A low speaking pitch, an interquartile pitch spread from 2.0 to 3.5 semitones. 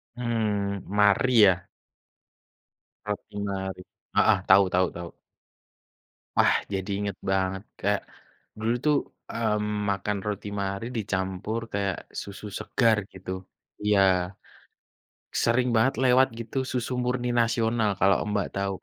Yes: low, 105 Hz; average, 2.8 semitones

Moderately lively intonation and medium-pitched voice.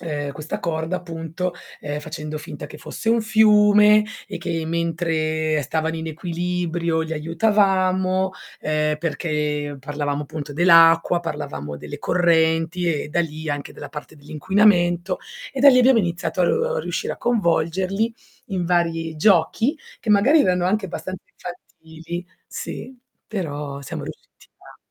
Yes: average, 3.3 semitones; medium, 170 Hz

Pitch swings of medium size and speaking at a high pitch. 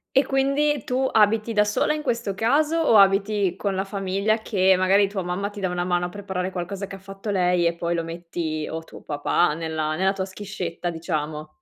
Yes: average, 3.1 semitones; high, 195 Hz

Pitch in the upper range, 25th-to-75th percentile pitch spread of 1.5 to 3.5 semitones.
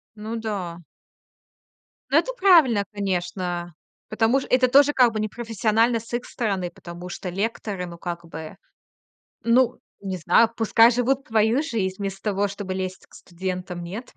No: high, 205 Hz; average, 4.2 semitones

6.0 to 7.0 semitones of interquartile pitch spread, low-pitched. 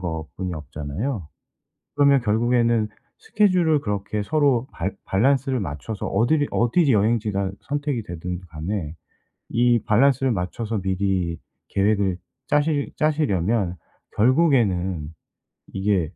Yes: wide, 6.3 semitones; low, 105 Hz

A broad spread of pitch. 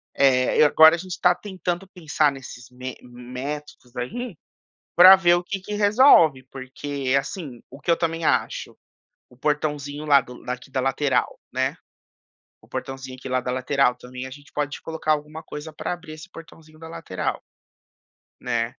No: average, 4.2 semitones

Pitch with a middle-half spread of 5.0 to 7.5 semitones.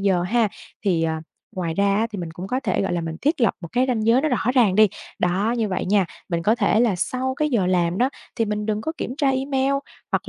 Yes: wide, 5.5 semitones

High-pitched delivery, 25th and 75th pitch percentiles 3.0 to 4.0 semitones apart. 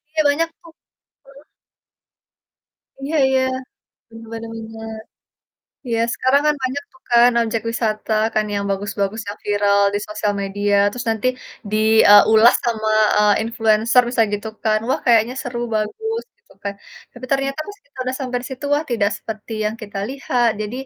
Yes: high, 225 Hz; average, 3.5 semitones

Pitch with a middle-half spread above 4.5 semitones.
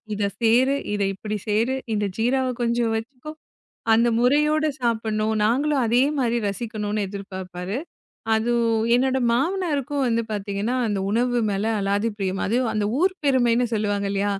No: average, 3.8 semitones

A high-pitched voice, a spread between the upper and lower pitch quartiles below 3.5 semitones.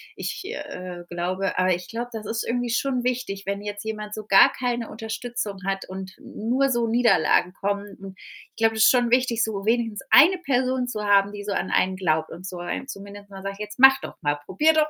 No: high, 210 Hz; average, 3.9 semitones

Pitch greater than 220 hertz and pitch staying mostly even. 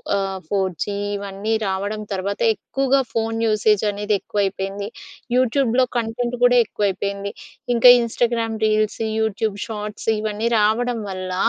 No: high, 215 Hz; narrow, 2.3 semitones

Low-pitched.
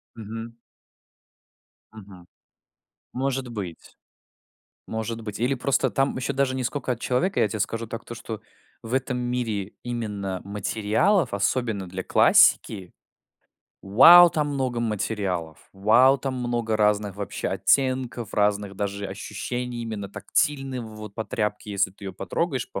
Yes: low, 115 Hz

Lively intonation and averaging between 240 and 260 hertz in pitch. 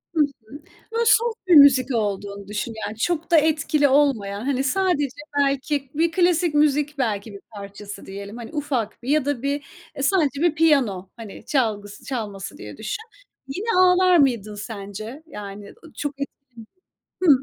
No: wide, 6.5 semitones; very high, 270 Hz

